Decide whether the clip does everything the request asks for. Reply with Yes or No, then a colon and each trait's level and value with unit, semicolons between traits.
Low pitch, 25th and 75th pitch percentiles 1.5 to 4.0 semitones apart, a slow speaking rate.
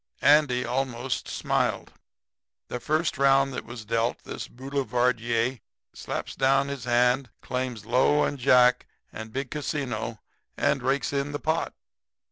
Yes: low, 130 Hz; narrow, 2.4 semitones; slow, 130 wpm